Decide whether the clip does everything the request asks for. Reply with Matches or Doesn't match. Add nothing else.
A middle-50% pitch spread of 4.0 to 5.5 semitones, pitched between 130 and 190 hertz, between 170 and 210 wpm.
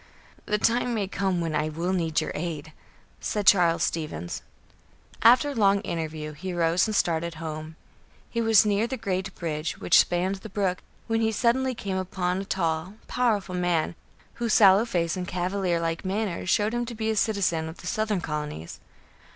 Matches